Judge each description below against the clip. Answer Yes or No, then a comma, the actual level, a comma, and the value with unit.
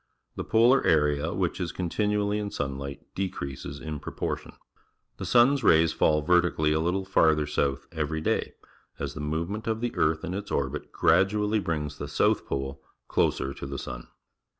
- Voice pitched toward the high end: No, very low, 80 Hz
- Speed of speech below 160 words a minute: No, average, 175 wpm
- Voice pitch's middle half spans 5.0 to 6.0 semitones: Yes, wide, 5.5 semitones